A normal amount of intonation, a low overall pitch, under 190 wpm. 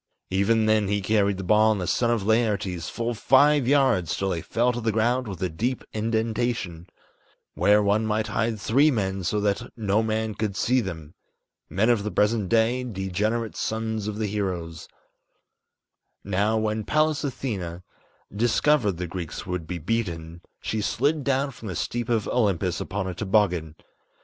Yes: average, 3.4 semitones; low, 105 Hz; average, 170 wpm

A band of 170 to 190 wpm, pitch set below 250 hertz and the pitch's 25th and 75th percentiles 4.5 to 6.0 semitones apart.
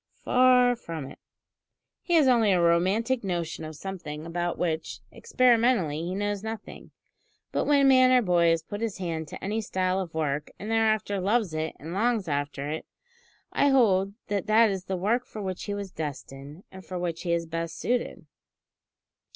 Yes: average, 180 wpm; high, 190 Hz; average, 5.2 semitones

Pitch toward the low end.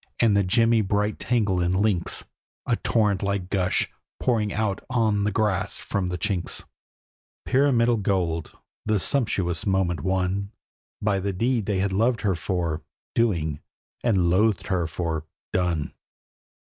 Yes: low, 100 Hz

